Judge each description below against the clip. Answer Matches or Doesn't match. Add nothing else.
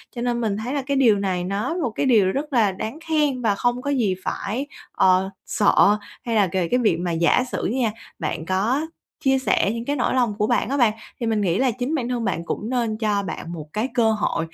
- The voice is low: Doesn't match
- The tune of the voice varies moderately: Matches